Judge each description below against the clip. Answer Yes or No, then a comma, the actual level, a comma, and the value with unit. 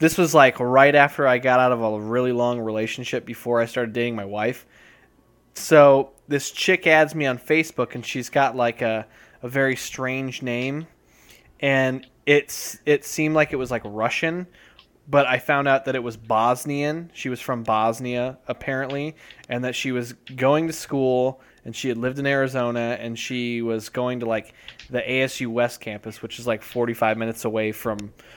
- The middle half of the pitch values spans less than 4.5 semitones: Yes, average, 2.8 semitones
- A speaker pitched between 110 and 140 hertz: Yes, low, 125 Hz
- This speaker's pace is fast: No, average, 185 wpm